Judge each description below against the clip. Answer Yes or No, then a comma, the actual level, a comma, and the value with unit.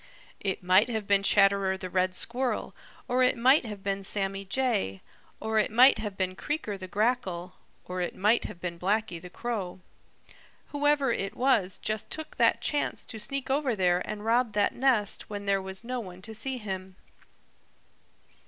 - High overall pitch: Yes, high, 205 Hz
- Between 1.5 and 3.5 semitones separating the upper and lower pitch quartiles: No, average, 4.3 semitones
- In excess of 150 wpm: Yes, average, 175 wpm